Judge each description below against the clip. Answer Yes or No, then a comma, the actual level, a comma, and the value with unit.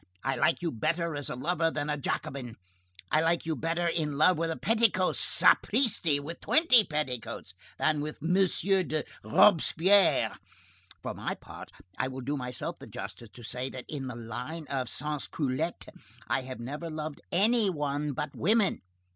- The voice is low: No, medium, 155 Hz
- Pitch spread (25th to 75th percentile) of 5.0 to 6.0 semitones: No, average, 4.3 semitones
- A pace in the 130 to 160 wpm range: No, average, 170 wpm